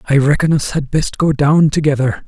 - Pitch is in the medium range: Yes, medium, 150 Hz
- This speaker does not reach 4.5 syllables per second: No, 5.3 syllables/s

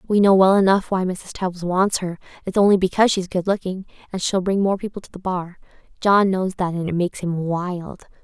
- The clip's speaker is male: No, female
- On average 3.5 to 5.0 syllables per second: No, 5.2 syllables/s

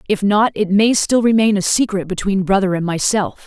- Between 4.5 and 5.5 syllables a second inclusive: Yes, 5.2 syllables/s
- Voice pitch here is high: Yes, high, 200 Hz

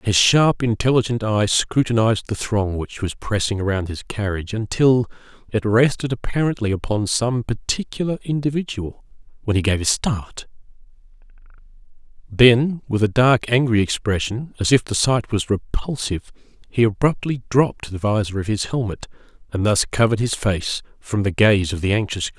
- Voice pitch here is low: Yes, low, 110 Hz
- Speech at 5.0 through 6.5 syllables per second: Yes, 5.1 syllables/s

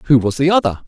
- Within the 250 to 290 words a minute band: Yes, fast, 275 wpm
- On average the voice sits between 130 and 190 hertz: Yes, medium, 140 Hz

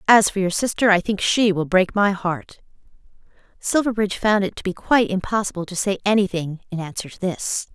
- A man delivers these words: No, female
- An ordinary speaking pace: Yes, average, 195 wpm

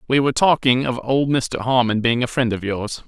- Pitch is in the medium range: No, low, 125 Hz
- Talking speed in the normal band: No, fast, 235 wpm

